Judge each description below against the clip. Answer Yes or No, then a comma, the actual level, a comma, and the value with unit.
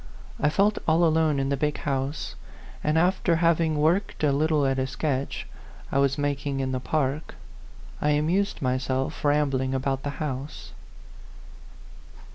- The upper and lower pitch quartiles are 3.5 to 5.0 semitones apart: No, average, 2.8 semitones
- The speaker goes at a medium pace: Yes, average, 155 wpm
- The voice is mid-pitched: Yes, medium, 145 Hz